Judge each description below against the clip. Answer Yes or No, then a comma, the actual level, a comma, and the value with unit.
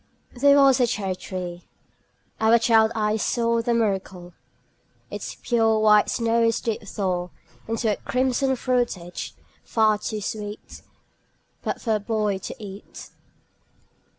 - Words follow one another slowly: Yes, slow, 125 wpm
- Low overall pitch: No, high, 220 Hz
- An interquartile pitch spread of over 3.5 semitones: No, narrow, 2.5 semitones